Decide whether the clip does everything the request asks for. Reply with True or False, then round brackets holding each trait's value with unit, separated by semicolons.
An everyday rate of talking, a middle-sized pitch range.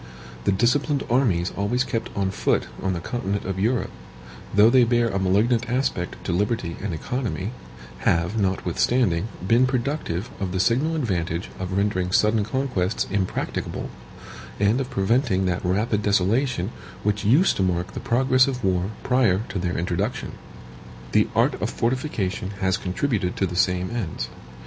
True (155 wpm; 4.8 semitones)